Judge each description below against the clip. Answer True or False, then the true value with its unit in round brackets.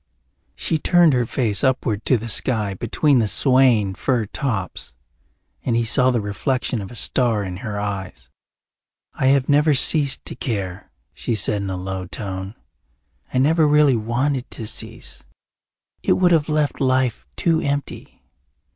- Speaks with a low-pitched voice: True (120 Hz)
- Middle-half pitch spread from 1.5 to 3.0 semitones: False (5.2 semitones)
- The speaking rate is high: False (155 wpm)